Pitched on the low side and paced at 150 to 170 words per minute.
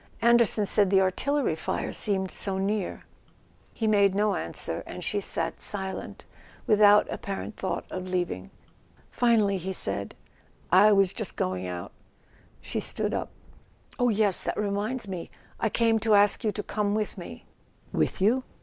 No: high, 205 Hz; average, 160 wpm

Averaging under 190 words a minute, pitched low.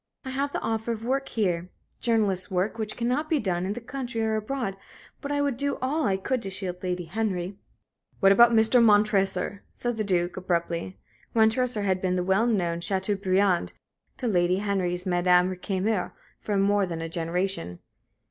No: average, 175 wpm; high, 200 Hz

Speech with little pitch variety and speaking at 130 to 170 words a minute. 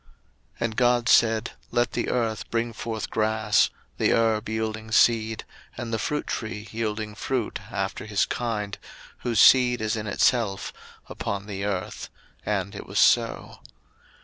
Yes: narrow, 1.8 semitones; average, 150 wpm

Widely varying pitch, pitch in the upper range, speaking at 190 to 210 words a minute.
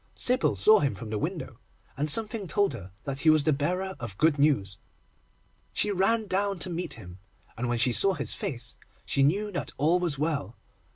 No: wide, 7.2 semitones; medium, 155 Hz; average, 195 wpm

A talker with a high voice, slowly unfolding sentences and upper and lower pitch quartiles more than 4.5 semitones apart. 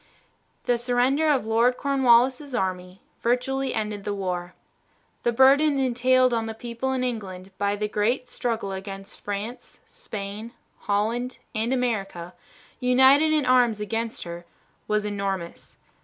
No: high, 230 Hz; slow, 130 wpm; average, 4.0 semitones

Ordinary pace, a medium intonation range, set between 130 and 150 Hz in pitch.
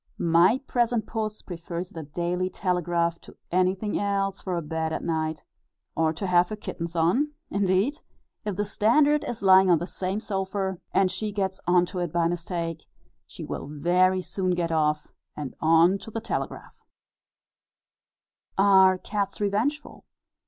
No: average, 155 wpm; average, 3.0 semitones; medium, 185 Hz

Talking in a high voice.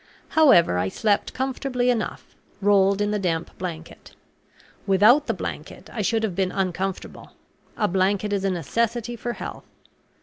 Yes: high, 205 Hz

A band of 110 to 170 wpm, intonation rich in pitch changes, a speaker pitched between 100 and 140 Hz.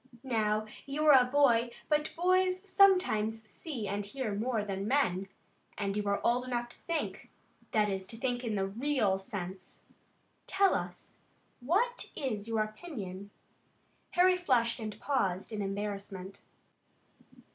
No: average, 145 wpm; wide, 6.1 semitones; high, 230 Hz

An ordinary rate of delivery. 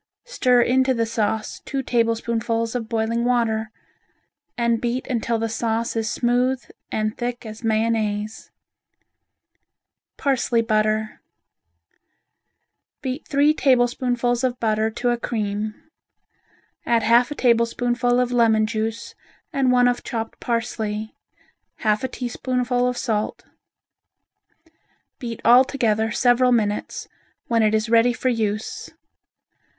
No: slow, 115 wpm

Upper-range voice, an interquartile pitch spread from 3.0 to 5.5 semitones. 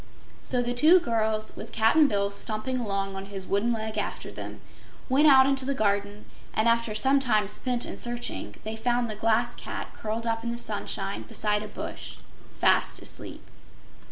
No: high, 225 Hz; narrow, 2.5 semitones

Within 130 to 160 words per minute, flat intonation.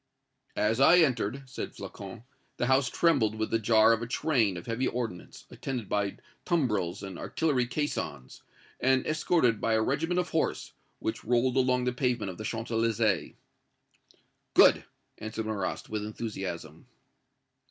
No: average, 150 wpm; average, 3.5 semitones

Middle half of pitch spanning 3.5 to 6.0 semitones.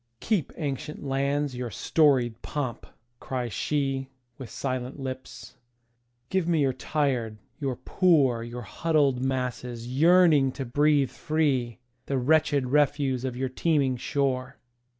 No: average, 2.8 semitones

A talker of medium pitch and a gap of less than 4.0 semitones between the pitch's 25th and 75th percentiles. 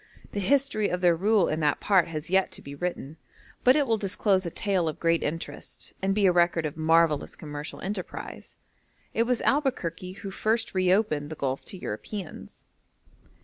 No: medium, 180 Hz; average, 4.3 semitones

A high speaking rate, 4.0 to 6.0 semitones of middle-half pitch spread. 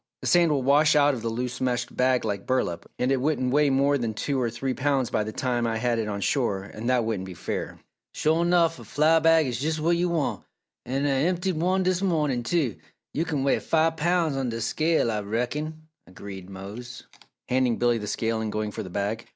Yes: fast, 225 wpm; wide, 5.5 semitones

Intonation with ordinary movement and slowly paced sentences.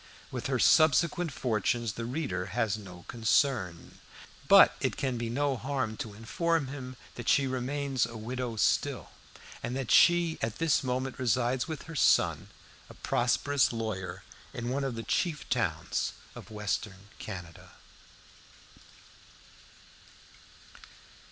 Yes: average, 4.0 semitones; slow, 130 wpm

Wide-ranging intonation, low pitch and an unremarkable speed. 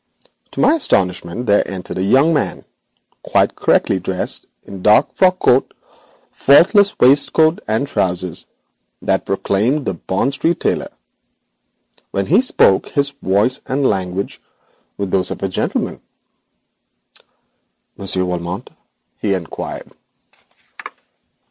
No: wide, 7.0 semitones; low, 100 Hz; slow, 115 wpm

